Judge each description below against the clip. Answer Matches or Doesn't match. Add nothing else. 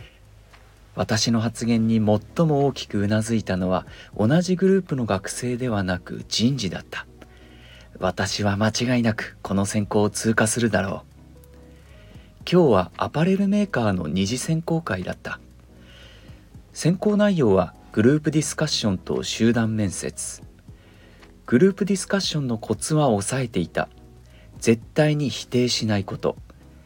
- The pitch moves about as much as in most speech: Doesn't match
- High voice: Doesn't match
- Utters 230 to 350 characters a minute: Matches